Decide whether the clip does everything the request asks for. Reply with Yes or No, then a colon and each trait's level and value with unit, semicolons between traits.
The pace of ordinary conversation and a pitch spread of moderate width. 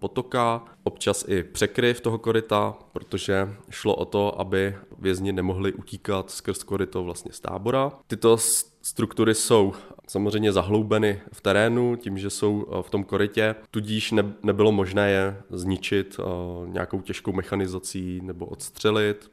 No: average, 130 wpm; narrow, 2.2 semitones